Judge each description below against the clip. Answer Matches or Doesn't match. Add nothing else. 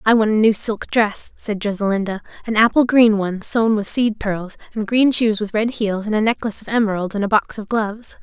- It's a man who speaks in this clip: Doesn't match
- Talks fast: Matches